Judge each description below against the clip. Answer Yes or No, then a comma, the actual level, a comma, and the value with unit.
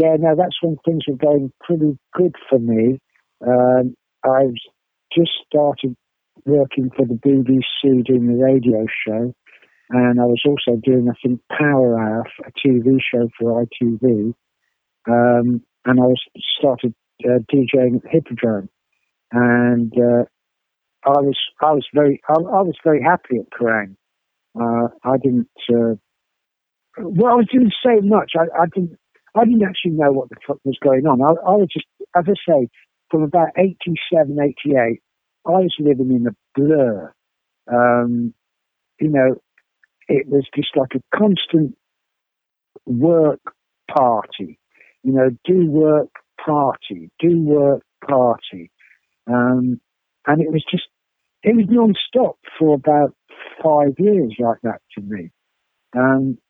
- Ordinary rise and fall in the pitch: Yes, average, 4.7 semitones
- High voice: No, low, 135 Hz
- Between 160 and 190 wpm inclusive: No, average, 145 wpm